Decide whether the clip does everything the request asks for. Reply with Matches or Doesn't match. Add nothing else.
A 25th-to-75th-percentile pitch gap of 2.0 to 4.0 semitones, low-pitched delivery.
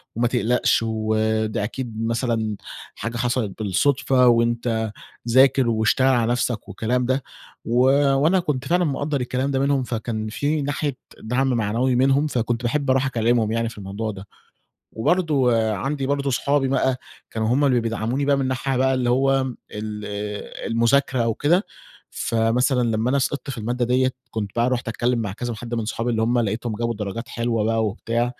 Matches